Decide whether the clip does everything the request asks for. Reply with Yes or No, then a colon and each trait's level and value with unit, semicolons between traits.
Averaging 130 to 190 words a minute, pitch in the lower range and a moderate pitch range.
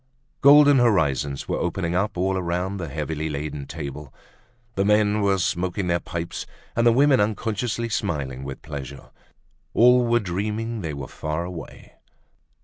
No: average, 145 wpm; very low, 90 Hz; wide, 5.9 semitones